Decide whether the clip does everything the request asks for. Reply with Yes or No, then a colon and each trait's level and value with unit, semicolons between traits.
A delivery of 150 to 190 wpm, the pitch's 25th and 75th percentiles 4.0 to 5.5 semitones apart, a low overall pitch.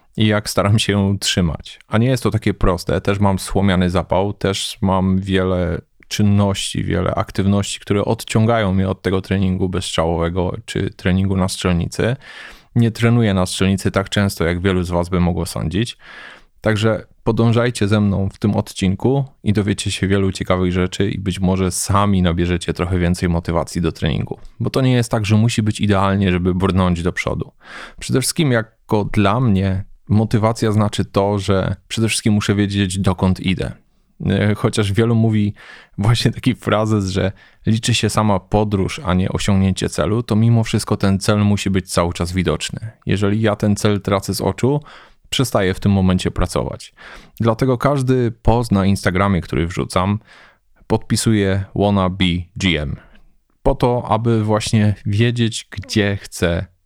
No: fast, 160 wpm; average, 2.8 semitones; low, 100 Hz